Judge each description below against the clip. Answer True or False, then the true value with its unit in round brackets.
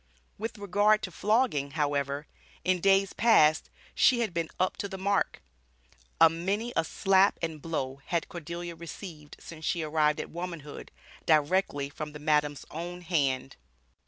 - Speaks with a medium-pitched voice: True (165 Hz)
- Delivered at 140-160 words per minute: True (150 wpm)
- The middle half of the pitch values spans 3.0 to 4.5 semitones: True (4.2 semitones)